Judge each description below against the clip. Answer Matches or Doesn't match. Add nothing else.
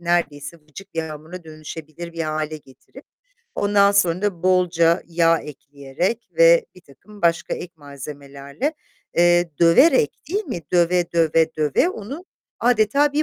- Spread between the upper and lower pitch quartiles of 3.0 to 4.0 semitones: Doesn't match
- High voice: Doesn't match